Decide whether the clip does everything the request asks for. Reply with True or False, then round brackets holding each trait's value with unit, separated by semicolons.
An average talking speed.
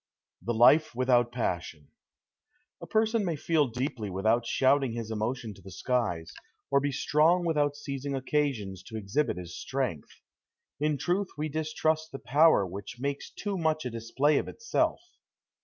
True (155 wpm)